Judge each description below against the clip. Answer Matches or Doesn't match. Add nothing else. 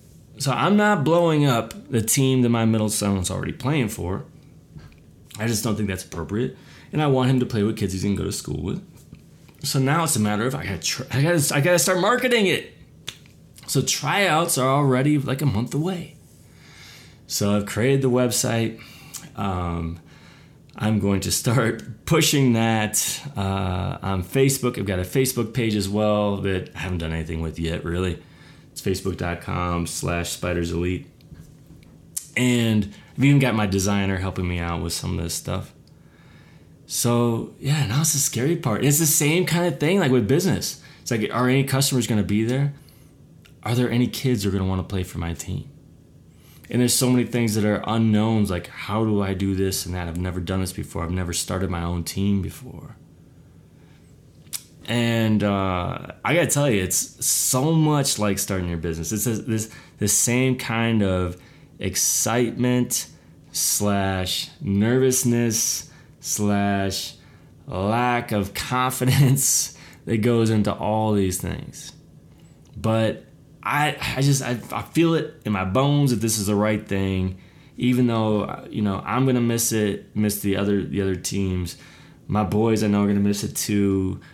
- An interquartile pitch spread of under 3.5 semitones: Doesn't match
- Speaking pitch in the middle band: Doesn't match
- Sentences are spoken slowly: Doesn't match